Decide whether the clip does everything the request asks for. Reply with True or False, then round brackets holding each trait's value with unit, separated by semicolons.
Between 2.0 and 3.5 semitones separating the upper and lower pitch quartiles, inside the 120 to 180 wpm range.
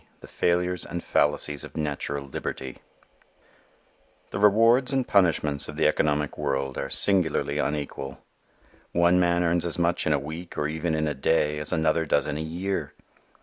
True (3.1 semitones; 165 wpm)